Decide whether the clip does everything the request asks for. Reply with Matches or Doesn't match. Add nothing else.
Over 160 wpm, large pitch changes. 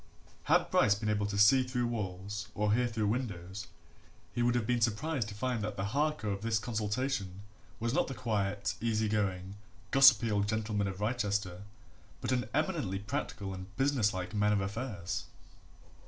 Doesn't match